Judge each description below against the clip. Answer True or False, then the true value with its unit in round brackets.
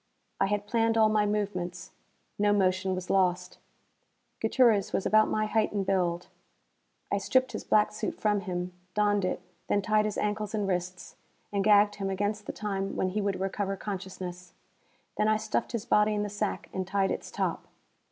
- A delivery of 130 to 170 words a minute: False (180 wpm)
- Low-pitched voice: False (205 Hz)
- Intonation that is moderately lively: False (2.0 semitones)